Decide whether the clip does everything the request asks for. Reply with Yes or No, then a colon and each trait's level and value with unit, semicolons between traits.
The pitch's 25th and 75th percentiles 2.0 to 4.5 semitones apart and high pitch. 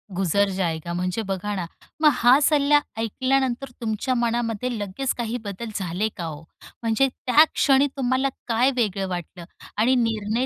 No: average, 5.0 semitones; high, 225 Hz